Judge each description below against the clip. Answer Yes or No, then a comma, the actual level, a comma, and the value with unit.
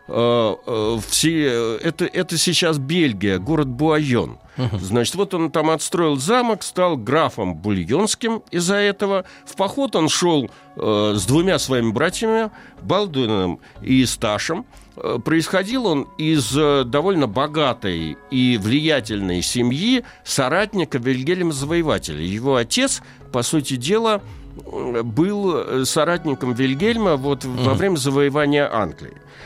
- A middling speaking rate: No, slow, 100 wpm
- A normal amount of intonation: No, wide, 6.6 semitones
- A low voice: No, medium, 145 Hz